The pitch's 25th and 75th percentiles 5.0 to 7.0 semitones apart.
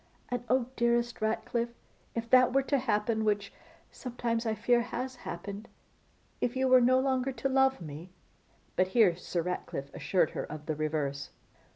Yes: wide, 5.5 semitones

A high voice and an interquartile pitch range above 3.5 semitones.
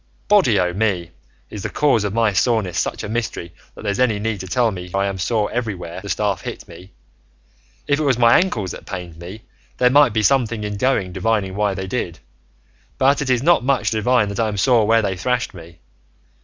No: low, 105 Hz; average, 4.2 semitones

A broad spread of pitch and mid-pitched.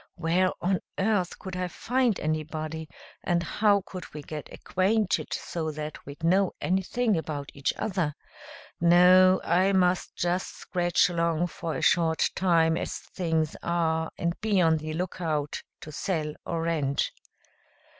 No: narrow, 2.6 semitones; medium, 170 Hz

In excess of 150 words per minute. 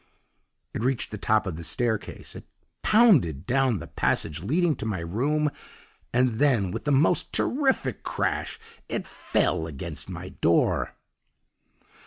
No: average, 140 wpm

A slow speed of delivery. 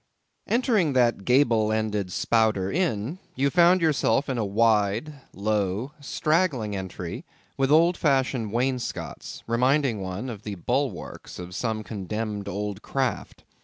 Yes: slow, 130 wpm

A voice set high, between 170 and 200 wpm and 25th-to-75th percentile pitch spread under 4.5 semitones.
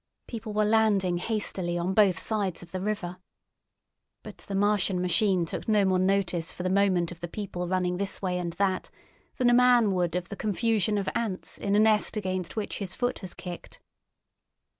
Yes: high, 195 Hz; average, 190 wpm; average, 2.9 semitones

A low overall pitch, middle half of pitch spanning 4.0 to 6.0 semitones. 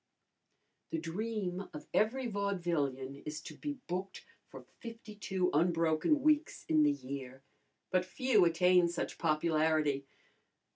No: medium, 175 Hz; average, 5.1 semitones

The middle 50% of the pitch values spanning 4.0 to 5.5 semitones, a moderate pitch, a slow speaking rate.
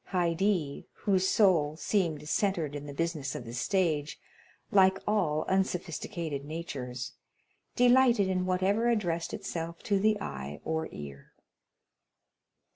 Yes: average, 4.7 semitones; medium, 170 Hz; slow, 120 wpm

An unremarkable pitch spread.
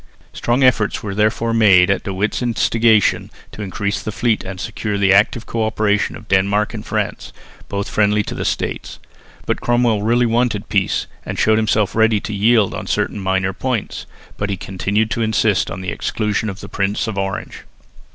No: narrow, 2.1 semitones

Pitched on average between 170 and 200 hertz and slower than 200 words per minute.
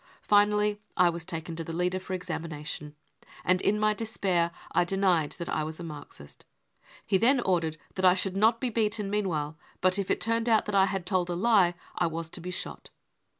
No: medium, 185 Hz; fast, 205 wpm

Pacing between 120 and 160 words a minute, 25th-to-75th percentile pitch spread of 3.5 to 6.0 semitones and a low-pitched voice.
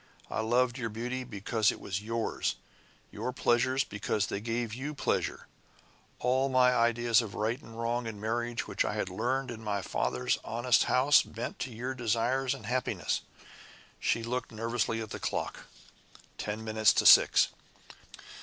No: average, 155 wpm; narrow, 2.4 semitones; low, 115 Hz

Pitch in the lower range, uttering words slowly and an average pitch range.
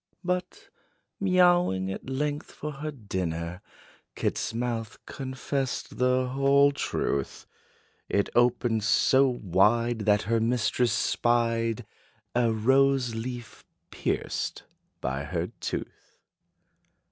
Yes: low, 120 Hz; slow, 100 wpm; average, 3.9 semitones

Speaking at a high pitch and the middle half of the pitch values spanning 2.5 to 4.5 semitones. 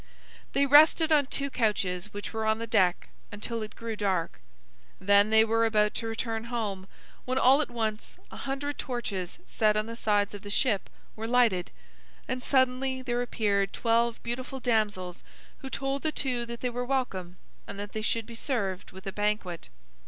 Yes: high, 225 Hz; average, 3.6 semitones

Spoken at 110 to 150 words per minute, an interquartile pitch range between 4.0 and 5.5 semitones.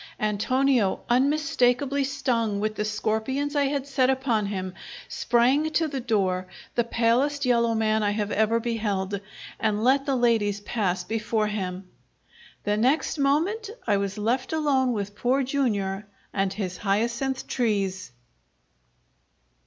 Yes: slow, 135 wpm; average, 4.5 semitones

